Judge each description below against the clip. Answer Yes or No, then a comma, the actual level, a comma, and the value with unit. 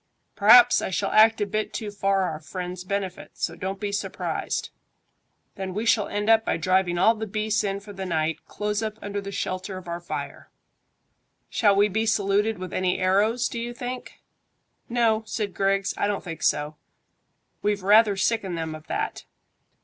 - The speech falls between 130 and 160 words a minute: No, average, 180 wpm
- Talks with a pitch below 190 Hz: No, high, 200 Hz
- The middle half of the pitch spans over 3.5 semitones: No, narrow, 2.6 semitones